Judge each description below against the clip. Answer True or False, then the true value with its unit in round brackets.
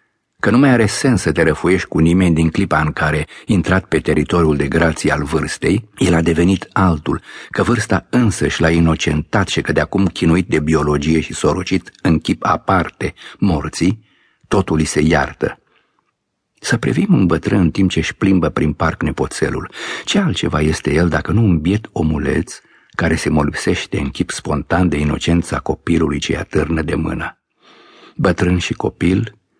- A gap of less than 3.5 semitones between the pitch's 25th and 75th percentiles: True (3.0 semitones)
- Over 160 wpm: True (170 wpm)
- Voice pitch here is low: True (85 Hz)